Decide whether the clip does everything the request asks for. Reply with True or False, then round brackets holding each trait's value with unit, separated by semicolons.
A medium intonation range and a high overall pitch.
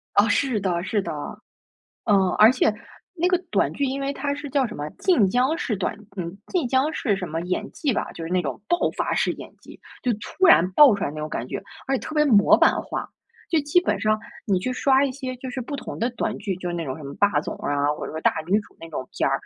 False (7.3 semitones; 220 Hz)